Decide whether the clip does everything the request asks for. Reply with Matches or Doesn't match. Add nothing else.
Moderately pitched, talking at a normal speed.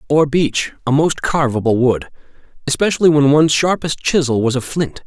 Matches